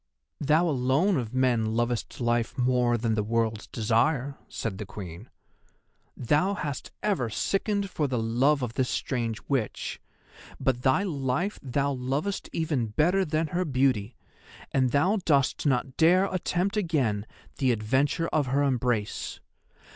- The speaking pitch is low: Yes, low, 130 Hz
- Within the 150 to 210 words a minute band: No, average, 140 wpm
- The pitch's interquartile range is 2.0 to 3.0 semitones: No, average, 4.7 semitones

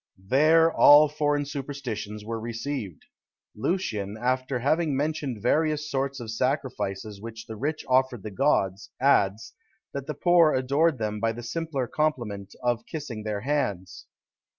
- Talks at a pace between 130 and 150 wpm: Yes, average, 140 wpm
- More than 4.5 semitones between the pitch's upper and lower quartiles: Yes, average, 5.2 semitones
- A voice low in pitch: Yes, low, 130 Hz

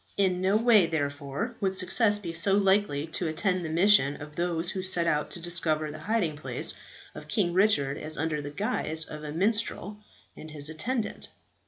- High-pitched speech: No, medium, 170 Hz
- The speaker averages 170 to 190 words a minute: Yes, average, 185 wpm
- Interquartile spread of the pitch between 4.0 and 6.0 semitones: Yes, average, 4.4 semitones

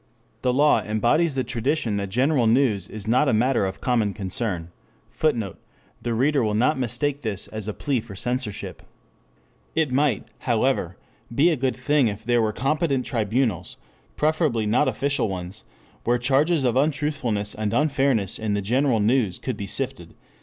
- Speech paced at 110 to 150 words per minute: No, average, 165 wpm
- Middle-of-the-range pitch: No, low, 120 Hz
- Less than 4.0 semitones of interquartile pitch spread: No, average, 4.5 semitones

